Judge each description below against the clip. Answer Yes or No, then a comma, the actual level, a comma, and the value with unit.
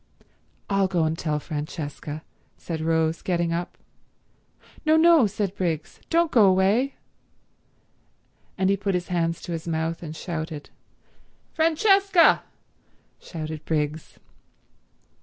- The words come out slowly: Yes, slow, 115 wpm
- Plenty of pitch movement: No, average, 4.2 semitones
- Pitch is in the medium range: Yes, medium, 175 Hz